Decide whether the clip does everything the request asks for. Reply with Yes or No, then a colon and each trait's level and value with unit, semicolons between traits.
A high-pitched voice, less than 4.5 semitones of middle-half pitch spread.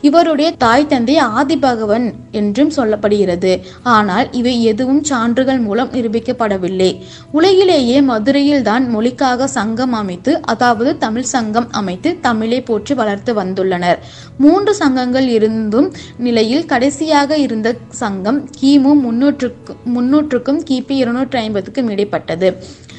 Yes: very high, 250 Hz; average, 4.1 semitones